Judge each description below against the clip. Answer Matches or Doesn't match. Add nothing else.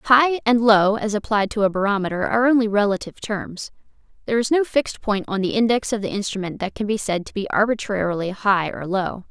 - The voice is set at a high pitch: Matches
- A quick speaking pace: Matches